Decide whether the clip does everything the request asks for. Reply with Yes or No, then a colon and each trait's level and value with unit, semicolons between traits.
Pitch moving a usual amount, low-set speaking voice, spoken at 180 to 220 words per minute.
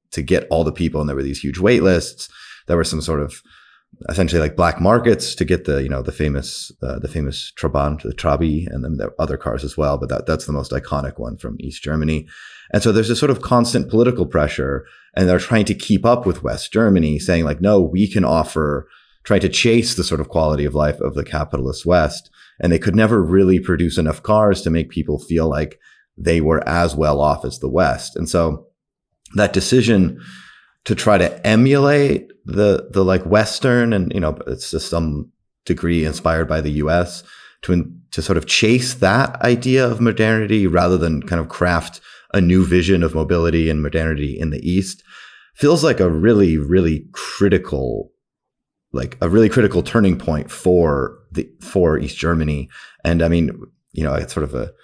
Yes: average, 4.2 semitones; very low, 85 Hz; average, 200 wpm